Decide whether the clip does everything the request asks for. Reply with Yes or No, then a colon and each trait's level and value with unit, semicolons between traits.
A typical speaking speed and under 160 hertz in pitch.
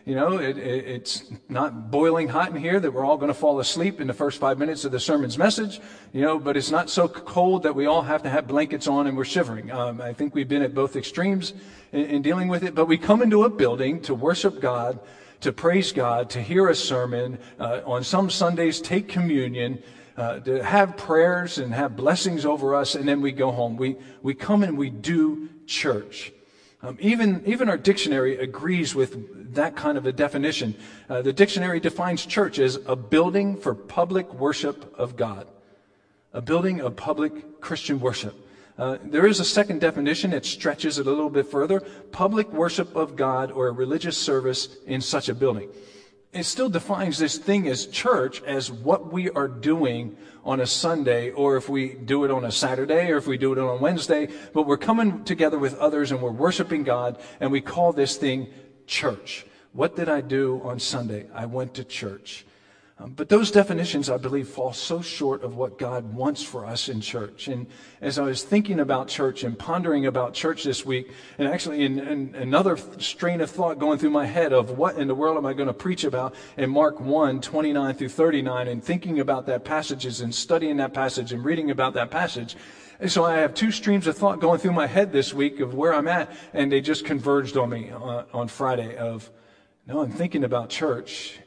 No: fast, 210 wpm; medium, 140 Hz